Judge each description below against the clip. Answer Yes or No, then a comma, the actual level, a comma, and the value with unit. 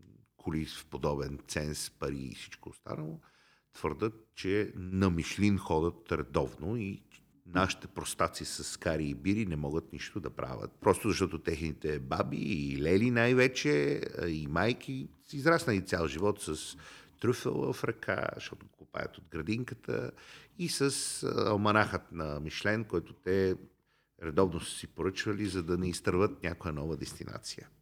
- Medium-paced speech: Yes, average, 140 wpm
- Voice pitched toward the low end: Yes, very low, 90 Hz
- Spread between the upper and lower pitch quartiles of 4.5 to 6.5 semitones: Yes, wide, 5.4 semitones